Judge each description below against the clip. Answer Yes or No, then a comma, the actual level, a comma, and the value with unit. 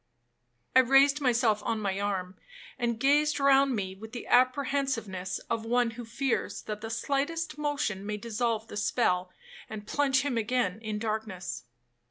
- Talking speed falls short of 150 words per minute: No, average, 155 wpm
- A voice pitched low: No, high, 230 Hz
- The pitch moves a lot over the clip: No, average, 4.4 semitones